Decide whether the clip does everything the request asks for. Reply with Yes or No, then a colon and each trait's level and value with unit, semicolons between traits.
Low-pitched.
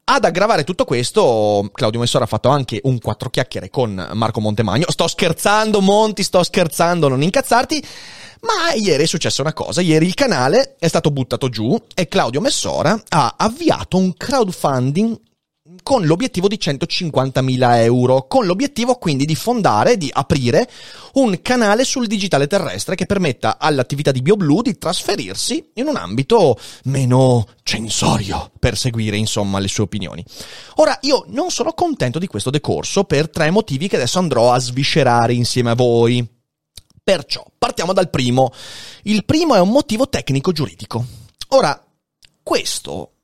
No: medium, 150 Hz